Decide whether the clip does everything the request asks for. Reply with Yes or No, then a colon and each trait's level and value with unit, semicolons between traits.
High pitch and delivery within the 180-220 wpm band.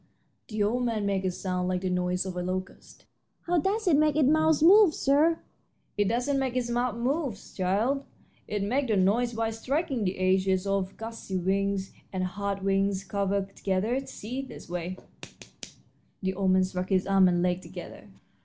Yes: high, 200 Hz; average, 190 wpm